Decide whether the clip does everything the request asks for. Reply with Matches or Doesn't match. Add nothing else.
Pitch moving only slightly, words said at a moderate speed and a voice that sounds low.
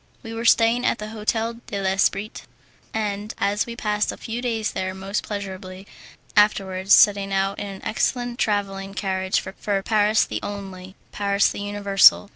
Doesn't match